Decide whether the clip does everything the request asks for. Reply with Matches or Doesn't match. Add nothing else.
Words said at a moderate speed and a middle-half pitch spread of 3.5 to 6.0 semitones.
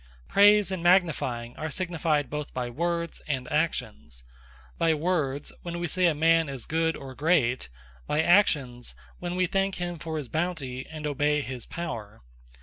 Matches